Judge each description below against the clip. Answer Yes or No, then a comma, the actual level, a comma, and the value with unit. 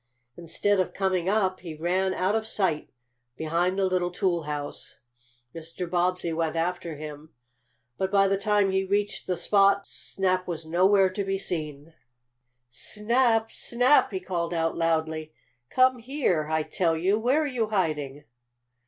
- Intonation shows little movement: No, average, 3.4 semitones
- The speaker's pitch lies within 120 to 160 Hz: No, medium, 185 Hz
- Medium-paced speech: Yes, average, 150 wpm